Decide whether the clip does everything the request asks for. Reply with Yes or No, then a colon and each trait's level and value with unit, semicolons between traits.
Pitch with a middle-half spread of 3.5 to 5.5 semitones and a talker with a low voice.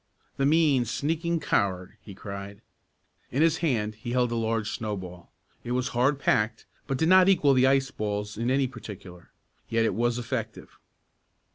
Yes: average, 4.5 semitones; low, 120 Hz